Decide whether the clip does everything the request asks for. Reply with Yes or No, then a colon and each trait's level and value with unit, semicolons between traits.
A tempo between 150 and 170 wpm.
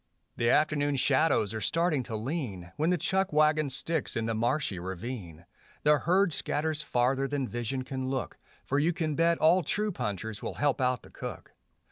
No: average, 180 wpm